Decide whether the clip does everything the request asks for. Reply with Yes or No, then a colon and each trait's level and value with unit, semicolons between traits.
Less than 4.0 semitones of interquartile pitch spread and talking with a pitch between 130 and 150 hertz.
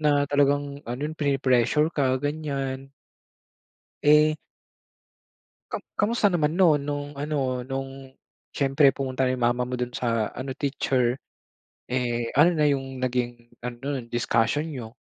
Yes: average, 2.8 semitones; low, 135 Hz